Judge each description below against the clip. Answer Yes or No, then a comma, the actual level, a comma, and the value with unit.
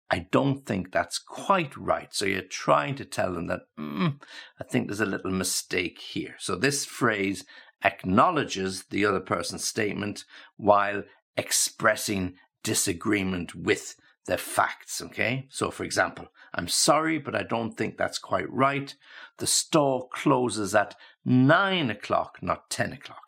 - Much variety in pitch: Yes, wide, 5.8 semitones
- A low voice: Yes, low, 110 Hz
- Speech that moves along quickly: No, average, 145 wpm